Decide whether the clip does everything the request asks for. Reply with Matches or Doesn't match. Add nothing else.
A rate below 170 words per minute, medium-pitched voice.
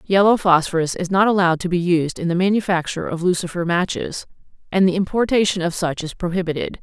Doesn't match